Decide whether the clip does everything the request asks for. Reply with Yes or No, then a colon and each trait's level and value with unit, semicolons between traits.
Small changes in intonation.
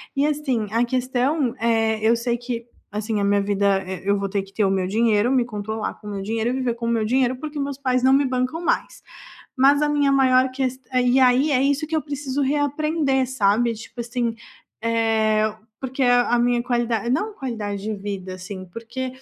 No: average, 3.5 semitones